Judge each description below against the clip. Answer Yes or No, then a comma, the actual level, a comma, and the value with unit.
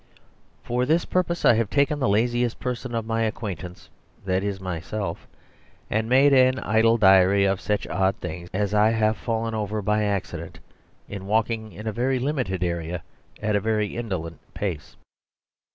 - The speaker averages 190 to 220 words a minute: No, average, 165 wpm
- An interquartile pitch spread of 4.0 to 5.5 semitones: No, average, 3.5 semitones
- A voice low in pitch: Yes, low, 105 Hz